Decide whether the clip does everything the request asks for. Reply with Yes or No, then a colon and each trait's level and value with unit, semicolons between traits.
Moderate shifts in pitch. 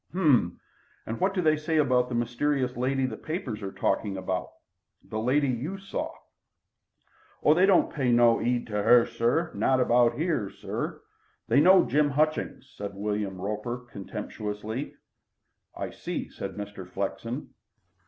No: wide, 5.8 semitones